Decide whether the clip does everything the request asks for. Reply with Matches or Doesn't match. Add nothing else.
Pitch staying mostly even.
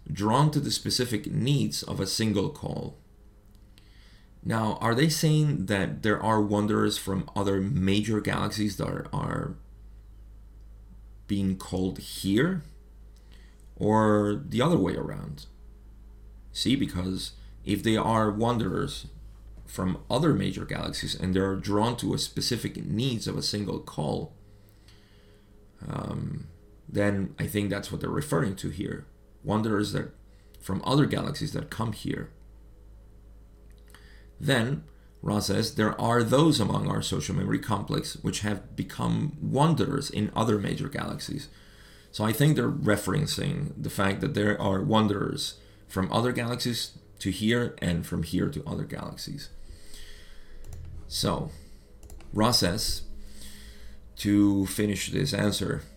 Matches